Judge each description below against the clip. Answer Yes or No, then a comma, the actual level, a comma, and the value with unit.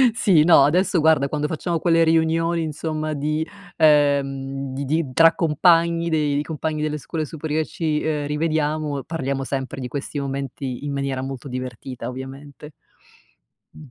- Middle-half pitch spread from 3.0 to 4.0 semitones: No, narrow, 2.6 semitones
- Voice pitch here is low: No, medium, 150 Hz